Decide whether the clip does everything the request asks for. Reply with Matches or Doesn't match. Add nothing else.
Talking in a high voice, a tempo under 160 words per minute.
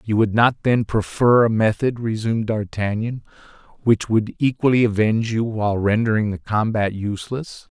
Doesn't match